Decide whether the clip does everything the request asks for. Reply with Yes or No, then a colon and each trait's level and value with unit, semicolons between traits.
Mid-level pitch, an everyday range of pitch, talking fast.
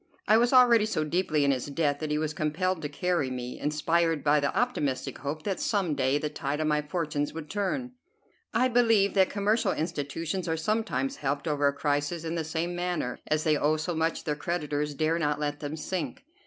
Yes: medium, 155 Hz; average, 3.6 semitones; fast, 210 wpm